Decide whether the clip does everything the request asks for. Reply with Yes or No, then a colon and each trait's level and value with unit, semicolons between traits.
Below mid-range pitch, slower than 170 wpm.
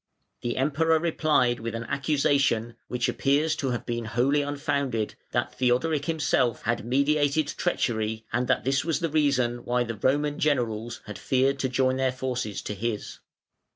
Yes: low, 130 Hz; average, 160 wpm